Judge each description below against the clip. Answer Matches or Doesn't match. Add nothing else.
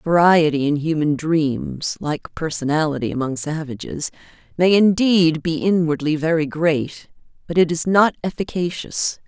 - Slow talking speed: Matches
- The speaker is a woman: Matches